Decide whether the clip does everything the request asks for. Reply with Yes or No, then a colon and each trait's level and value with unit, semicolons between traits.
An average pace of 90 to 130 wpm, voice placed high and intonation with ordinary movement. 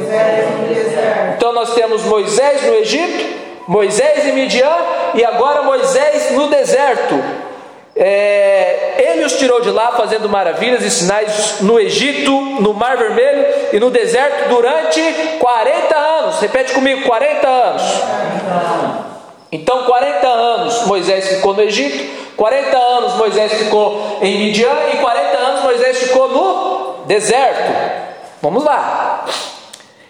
Yes: slow, 120 wpm; high, 235 Hz; average, 4.8 semitones